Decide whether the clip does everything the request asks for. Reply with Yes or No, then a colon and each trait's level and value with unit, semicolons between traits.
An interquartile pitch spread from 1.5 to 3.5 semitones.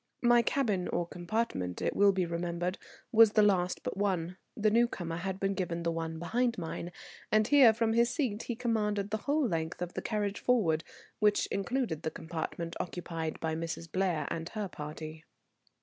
No: average, 4.7 semitones